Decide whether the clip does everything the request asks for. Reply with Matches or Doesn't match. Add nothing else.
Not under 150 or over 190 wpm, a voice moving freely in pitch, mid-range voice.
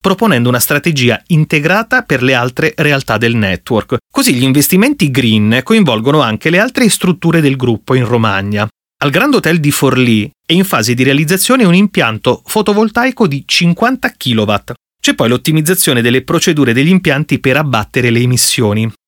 Matches